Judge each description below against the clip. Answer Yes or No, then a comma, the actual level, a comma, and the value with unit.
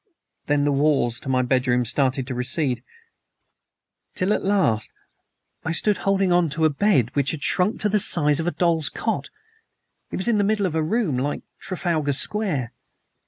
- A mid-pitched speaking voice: Yes, medium, 155 Hz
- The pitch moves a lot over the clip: Yes, wide, 6.0 semitones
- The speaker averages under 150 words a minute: No, average, 170 wpm